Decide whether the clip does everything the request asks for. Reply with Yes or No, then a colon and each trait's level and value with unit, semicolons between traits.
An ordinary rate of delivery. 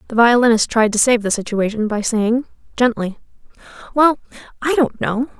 Yes: average, 155 wpm